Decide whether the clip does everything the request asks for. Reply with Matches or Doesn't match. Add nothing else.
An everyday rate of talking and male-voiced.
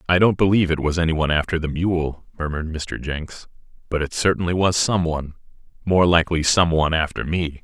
Matches